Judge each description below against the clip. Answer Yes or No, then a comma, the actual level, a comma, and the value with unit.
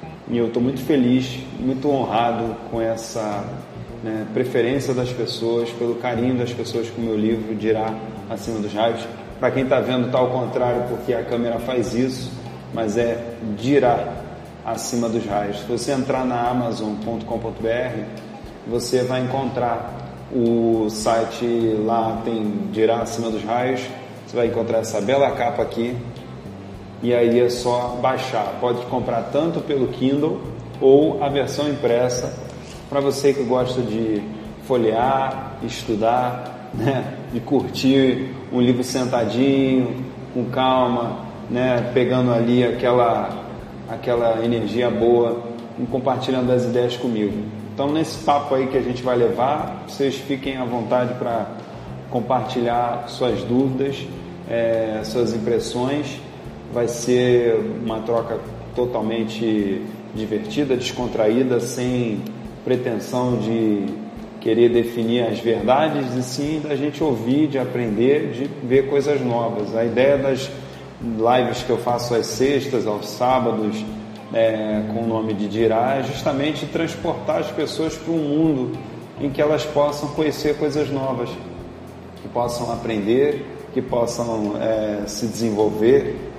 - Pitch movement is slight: Yes, narrow, 2.2 semitones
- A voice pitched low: Yes, low, 120 Hz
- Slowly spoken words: No, average, 135 wpm